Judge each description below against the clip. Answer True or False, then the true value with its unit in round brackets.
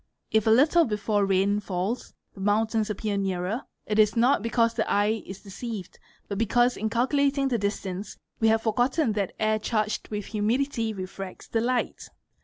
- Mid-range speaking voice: False (215 Hz)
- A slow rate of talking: False (170 wpm)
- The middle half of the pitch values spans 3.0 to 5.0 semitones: False (2.6 semitones)